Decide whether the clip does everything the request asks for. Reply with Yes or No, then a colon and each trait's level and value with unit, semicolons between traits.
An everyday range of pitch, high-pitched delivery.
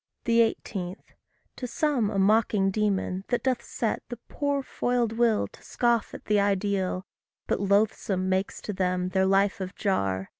Yes: average, 3.5 semitones; high, 205 Hz